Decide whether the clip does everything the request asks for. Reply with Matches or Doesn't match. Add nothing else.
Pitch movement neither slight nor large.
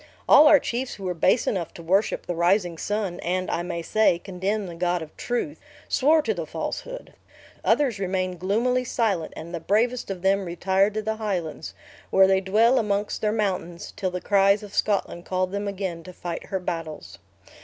Matches